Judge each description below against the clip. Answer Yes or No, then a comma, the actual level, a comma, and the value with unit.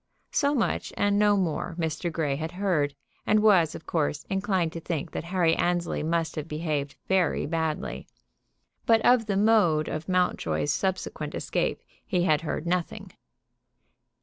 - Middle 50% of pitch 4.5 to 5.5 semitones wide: No, average, 3.7 semitones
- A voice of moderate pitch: Yes, medium, 170 Hz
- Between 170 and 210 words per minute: No, average, 150 wpm